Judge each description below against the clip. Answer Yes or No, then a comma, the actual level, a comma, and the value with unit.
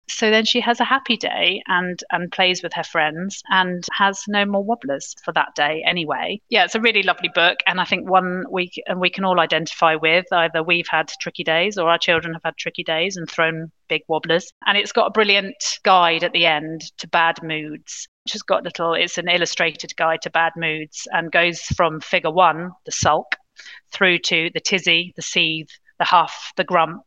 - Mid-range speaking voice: Yes, medium, 175 Hz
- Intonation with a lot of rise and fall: No, narrow, 2.6 semitones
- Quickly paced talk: Yes, fast, 210 wpm